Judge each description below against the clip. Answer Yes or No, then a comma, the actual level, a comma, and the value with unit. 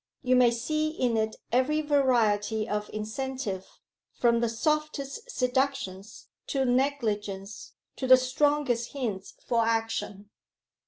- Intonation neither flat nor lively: Yes, average, 4.0 semitones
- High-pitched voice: Yes, high, 245 Hz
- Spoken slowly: Yes, slow, 115 wpm